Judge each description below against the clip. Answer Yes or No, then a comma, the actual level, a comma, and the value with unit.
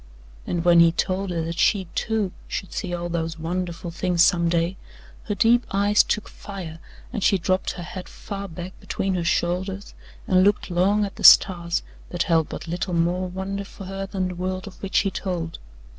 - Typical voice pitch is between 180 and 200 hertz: Yes, medium, 185 Hz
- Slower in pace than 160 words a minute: No, average, 195 wpm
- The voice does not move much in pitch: Yes, narrow, 2.2 semitones